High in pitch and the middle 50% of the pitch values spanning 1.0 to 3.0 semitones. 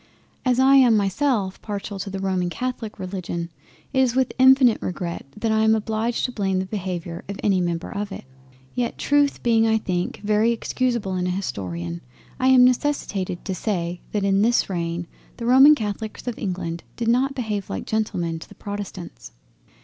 No: high, 205 Hz; average, 4.7 semitones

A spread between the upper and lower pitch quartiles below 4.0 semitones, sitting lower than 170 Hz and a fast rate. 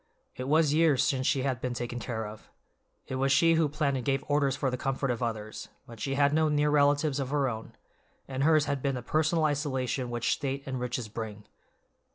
Yes: average, 2.8 semitones; low, 135 Hz; fast, 215 wpm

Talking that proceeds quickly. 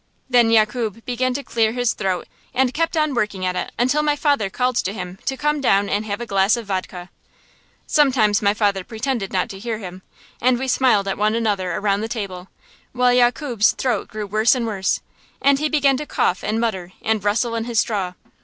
Yes: fast, 210 wpm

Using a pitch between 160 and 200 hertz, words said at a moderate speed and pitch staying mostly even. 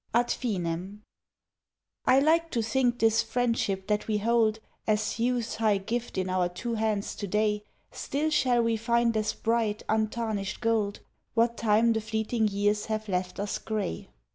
No: high, 220 Hz; average, 160 wpm; narrow, 2.1 semitones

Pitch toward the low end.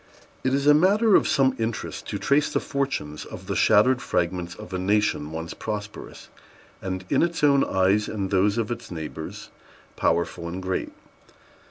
Yes: low, 105 Hz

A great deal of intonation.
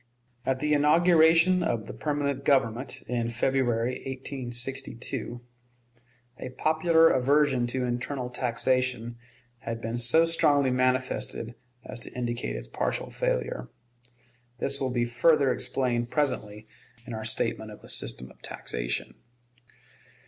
No: average, 3.2 semitones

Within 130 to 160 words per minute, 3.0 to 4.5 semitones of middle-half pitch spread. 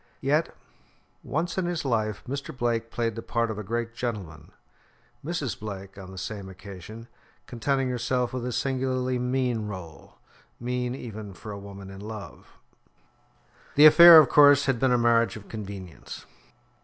Yes: average, 155 wpm; average, 4.1 semitones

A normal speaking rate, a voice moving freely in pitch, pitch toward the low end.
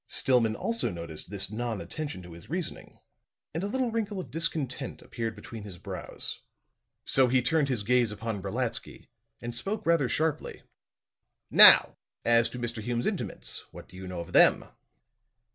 Yes: average, 160 wpm; wide, 6.5 semitones; low, 120 Hz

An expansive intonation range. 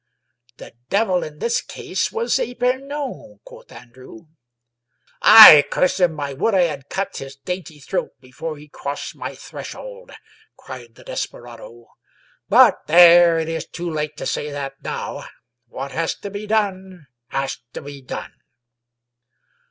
Yes: wide, 6.5 semitones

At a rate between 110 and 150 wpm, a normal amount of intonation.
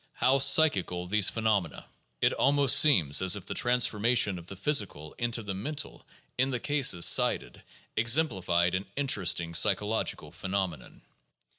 No: average, 145 wpm; wide, 5.8 semitones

